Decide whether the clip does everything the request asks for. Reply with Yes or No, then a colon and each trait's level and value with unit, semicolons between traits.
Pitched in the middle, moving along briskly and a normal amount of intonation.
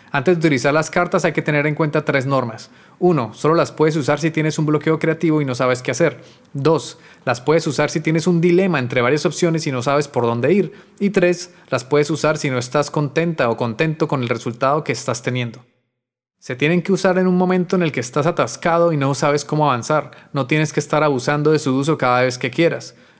Yes: medium, 150 Hz; fast, 235 wpm; average, 3.6 semitones